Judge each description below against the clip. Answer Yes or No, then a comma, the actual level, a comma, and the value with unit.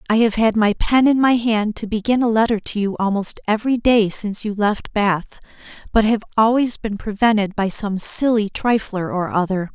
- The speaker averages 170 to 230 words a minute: Yes, average, 195 wpm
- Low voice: No, high, 215 Hz